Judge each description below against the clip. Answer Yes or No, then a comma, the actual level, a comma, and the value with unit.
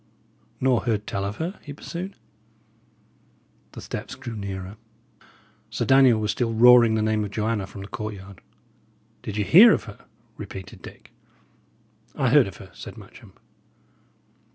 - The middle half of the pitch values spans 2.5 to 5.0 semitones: Yes, average, 4.2 semitones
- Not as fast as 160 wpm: Yes, average, 150 wpm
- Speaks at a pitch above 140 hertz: No, low, 110 Hz